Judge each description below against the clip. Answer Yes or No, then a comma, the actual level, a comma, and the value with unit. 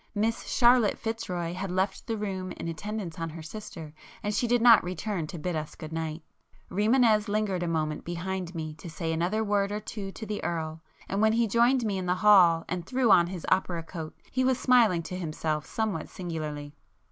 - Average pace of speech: No, fast, 210 wpm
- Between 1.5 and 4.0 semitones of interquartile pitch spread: No, average, 4.5 semitones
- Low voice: No, medium, 185 Hz